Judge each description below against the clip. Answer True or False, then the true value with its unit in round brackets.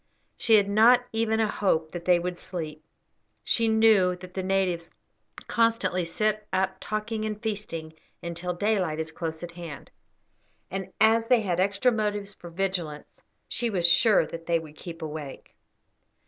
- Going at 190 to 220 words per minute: False (160 wpm)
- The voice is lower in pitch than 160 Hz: False (190 Hz)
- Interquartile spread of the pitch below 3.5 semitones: False (4.1 semitones)